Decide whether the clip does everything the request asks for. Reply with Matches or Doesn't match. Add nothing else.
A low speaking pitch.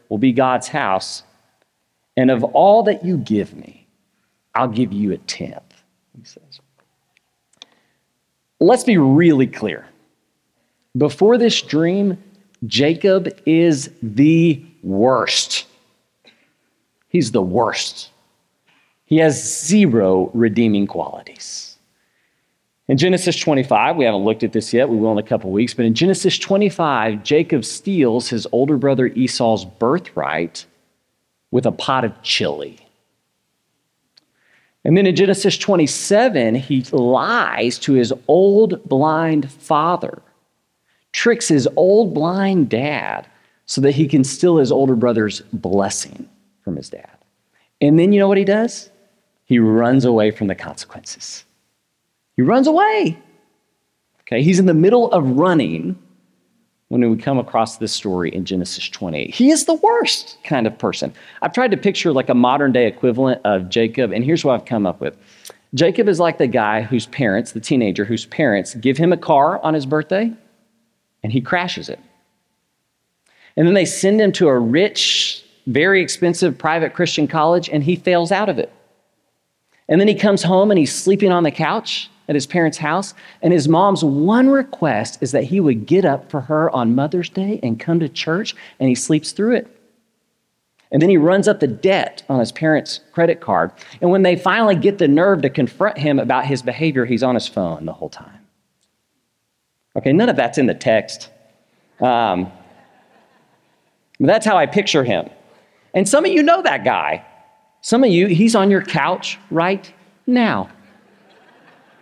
Doesn't match